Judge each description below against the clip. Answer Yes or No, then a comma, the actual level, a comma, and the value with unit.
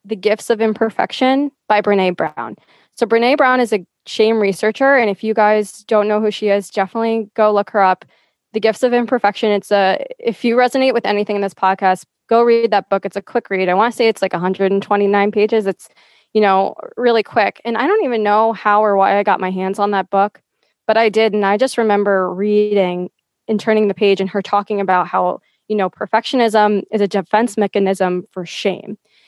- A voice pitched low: No, high, 210 Hz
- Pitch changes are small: Yes, narrow, 2.3 semitones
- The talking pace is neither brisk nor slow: No, fast, 215 wpm